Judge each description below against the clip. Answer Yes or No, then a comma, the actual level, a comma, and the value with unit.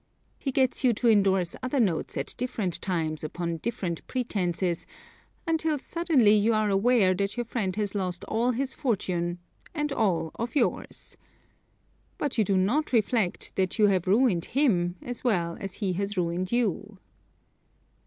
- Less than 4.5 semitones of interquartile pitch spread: No, average, 5.3 semitones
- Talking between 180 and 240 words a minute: No, average, 155 wpm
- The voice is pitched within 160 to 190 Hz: No, high, 205 Hz